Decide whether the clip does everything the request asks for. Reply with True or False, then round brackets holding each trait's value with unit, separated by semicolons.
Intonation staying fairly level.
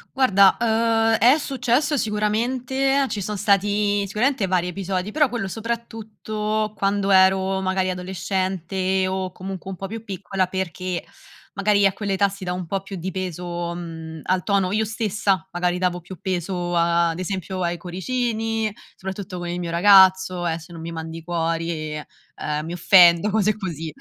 False (3.1 semitones)